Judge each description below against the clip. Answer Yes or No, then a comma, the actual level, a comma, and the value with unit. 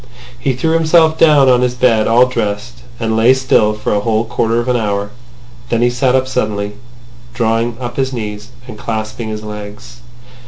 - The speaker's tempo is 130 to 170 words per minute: No, average, 185 wpm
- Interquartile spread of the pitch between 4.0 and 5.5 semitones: No, average, 2.8 semitones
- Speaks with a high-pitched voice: No, low, 120 Hz